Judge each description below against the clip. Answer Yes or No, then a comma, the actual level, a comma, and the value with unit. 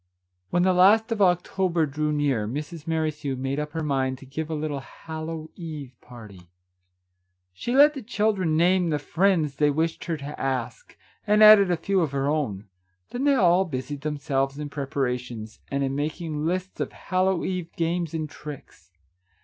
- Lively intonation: No, average, 4.5 semitones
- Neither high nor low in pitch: Yes, medium, 155 Hz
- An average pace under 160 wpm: No, average, 175 wpm